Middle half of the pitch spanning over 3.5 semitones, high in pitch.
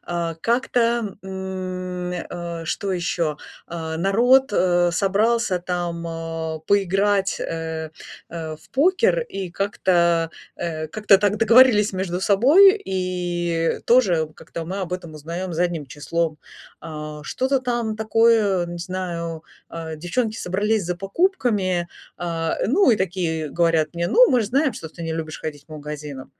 No: average, 4.2 semitones; medium, 180 Hz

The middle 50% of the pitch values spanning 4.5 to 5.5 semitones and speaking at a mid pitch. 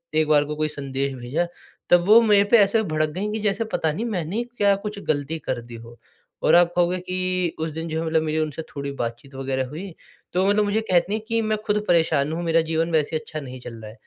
Yes: average, 5.2 semitones; medium, 160 Hz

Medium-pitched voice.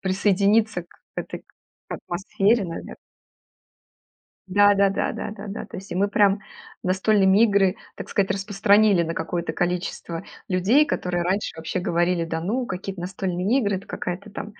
No: high, 195 Hz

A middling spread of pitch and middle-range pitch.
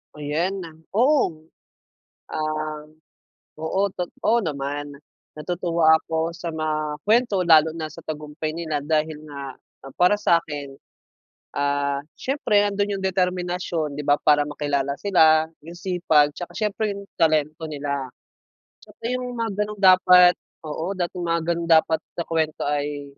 Yes: average, 3.5 semitones; medium, 160 Hz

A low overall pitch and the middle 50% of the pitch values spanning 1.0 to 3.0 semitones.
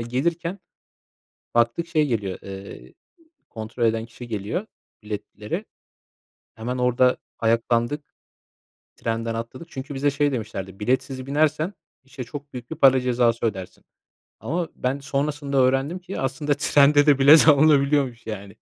No: low, 130 Hz; average, 4.0 semitones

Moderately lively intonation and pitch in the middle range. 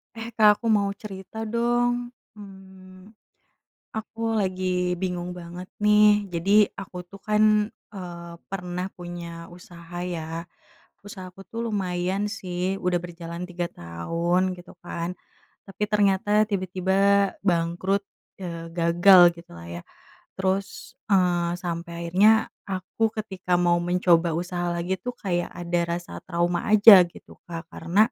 No: narrow, 2.3 semitones; medium, 180 Hz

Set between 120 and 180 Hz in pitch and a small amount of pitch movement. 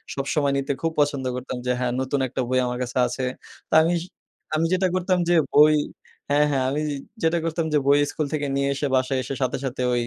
No: medium, 140 Hz; average, 3.2 semitones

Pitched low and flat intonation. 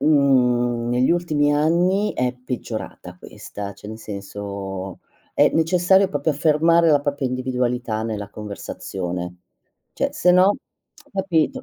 No: low, 130 Hz; wide, 7.3 semitones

